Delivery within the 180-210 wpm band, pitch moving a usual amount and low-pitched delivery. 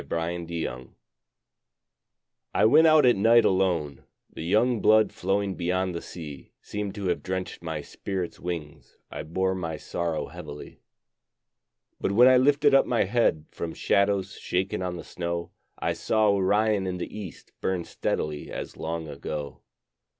No: average, 150 wpm; average, 4.0 semitones; very low, 95 Hz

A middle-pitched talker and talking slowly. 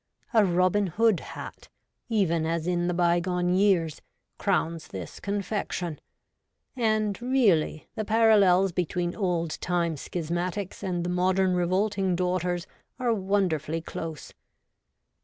Yes: medium, 180 Hz; slow, 130 wpm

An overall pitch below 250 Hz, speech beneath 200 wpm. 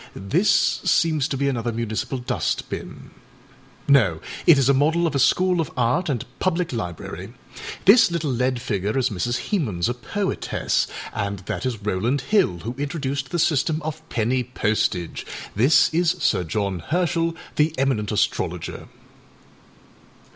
Yes: low, 135 Hz; average, 145 wpm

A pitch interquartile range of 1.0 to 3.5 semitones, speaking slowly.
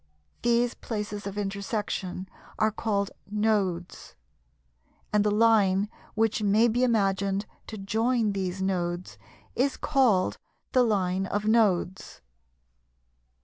Yes: narrow, 2.6 semitones; slow, 105 wpm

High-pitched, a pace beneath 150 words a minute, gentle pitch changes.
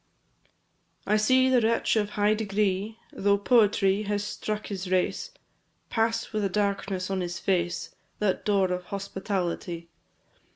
Yes: high, 200 Hz; slow, 135 wpm; narrow, 2.2 semitones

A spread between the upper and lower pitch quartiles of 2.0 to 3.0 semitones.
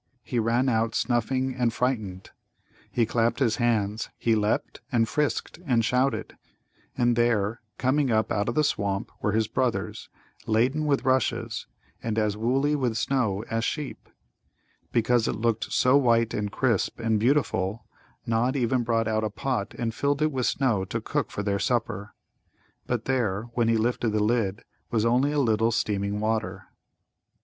Yes: average, 2.7 semitones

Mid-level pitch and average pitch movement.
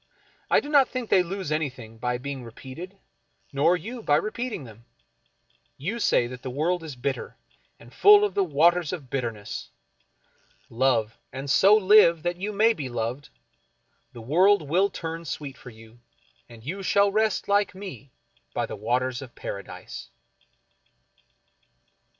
No: medium, 155 Hz; wide, 7.7 semitones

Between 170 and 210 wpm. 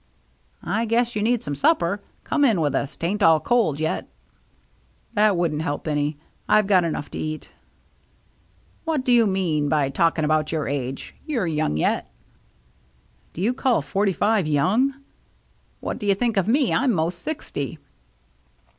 Yes: average, 175 wpm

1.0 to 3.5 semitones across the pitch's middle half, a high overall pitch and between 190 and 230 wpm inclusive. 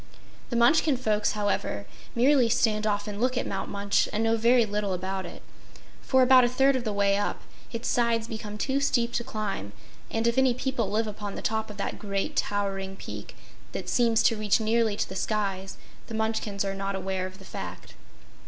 Yes: average, 2.9 semitones; high, 215 Hz; average, 200 wpm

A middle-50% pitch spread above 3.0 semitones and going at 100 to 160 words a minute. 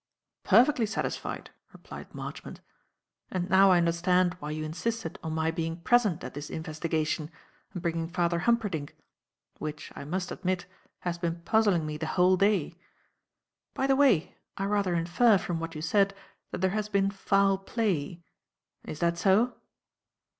Yes: average, 3.4 semitones; average, 155 wpm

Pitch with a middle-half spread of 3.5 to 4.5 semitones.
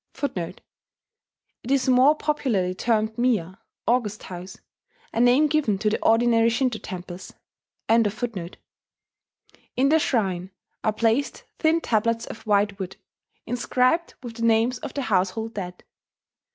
Yes: average, 4.0 semitones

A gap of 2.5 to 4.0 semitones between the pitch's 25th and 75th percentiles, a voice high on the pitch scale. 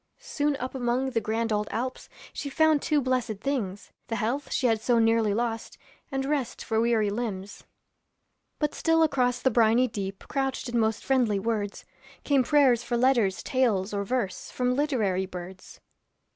Yes: average, 3.6 semitones; high, 235 Hz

